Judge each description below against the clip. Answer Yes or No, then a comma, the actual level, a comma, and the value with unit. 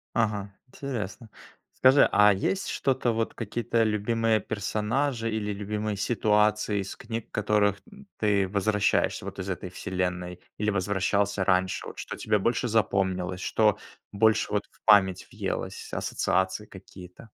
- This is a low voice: Yes, low, 105 Hz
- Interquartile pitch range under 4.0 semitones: Yes, narrow, 2.5 semitones